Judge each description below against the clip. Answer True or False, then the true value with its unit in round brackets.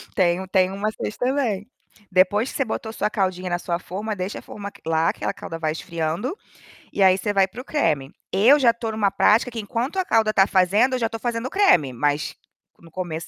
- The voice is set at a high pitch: True (200 Hz)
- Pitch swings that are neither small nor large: True (4.0 semitones)